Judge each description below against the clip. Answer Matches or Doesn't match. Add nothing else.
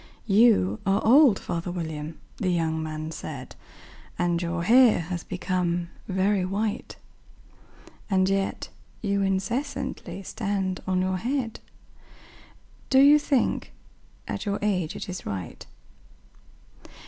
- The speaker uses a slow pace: Matches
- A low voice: Doesn't match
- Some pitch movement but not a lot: Matches